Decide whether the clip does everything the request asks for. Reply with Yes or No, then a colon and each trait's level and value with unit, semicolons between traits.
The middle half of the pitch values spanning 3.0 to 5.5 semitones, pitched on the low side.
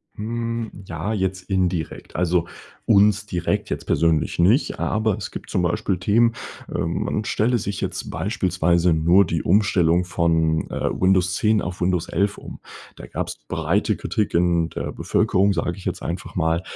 Yes: average, 3.3 semitones; very low, 90 Hz